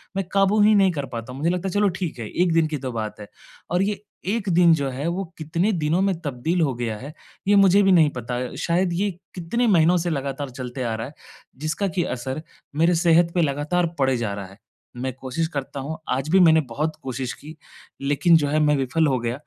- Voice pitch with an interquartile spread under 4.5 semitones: No, average, 5.1 semitones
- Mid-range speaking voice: Yes, medium, 155 Hz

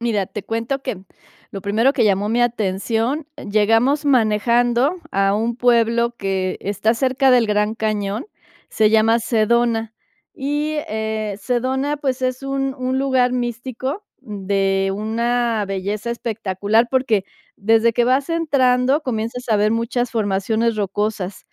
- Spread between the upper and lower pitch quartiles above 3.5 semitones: No, average, 3.2 semitones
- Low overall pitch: No, high, 230 Hz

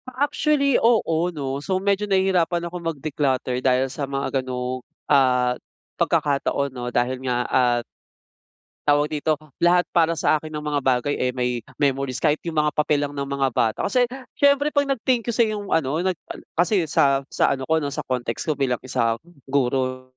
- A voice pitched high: No, medium, 145 Hz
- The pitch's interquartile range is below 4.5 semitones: No, wide, 5.4 semitones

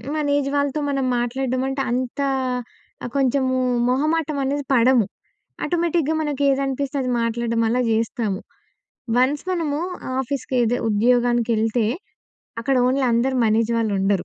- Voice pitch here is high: Yes, very high, 260 Hz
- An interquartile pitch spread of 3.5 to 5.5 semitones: No, average, 3.1 semitones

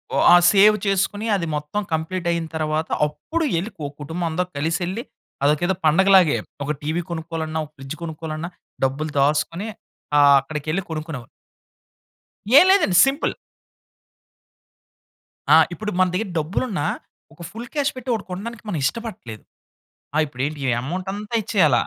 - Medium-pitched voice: Yes, medium, 170 Hz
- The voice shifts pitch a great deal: No, average, 4.6 semitones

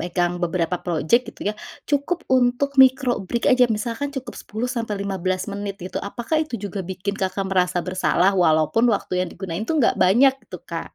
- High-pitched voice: Yes, high, 205 Hz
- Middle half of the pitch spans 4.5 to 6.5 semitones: Yes, wide, 5.4 semitones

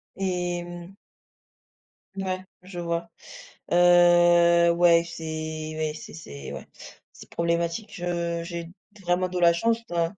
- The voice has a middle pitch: Yes, medium, 175 Hz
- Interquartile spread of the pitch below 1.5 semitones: Yes, narrow, 0.8 semitones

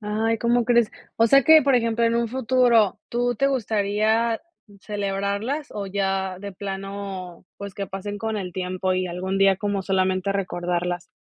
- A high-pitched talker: Yes, high, 200 Hz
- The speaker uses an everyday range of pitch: Yes, average, 3.3 semitones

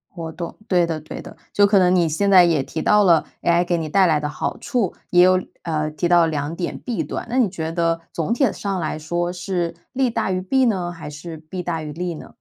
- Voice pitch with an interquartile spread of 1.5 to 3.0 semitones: Yes, narrow, 2.6 semitones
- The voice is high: No, medium, 175 Hz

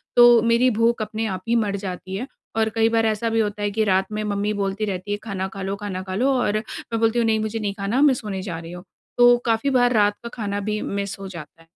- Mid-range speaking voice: No, high, 210 Hz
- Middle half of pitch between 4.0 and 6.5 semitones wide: No, narrow, 2.5 semitones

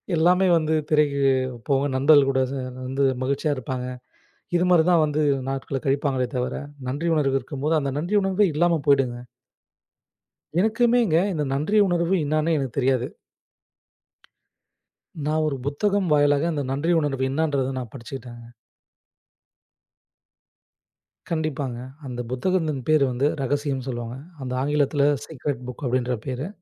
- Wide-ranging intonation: No, average, 3.3 semitones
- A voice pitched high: No, medium, 140 Hz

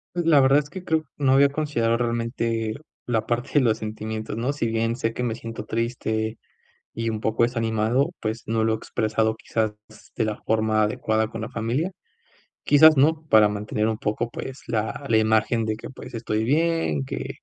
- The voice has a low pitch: Yes, low, 115 Hz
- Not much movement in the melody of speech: No, average, 3.1 semitones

